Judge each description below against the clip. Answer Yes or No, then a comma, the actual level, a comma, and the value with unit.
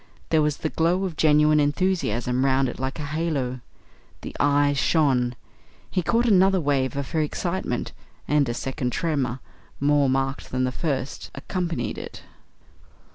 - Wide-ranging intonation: No, average, 3.7 semitones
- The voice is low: No, medium, 145 Hz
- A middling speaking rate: Yes, average, 150 wpm